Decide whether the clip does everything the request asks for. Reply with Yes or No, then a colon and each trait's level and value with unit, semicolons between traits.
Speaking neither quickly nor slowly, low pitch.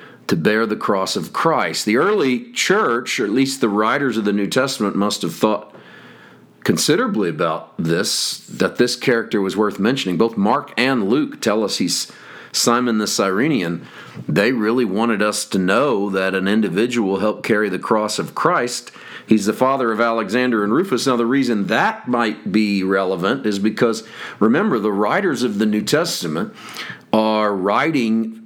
Yes: average, 170 wpm; low, 110 Hz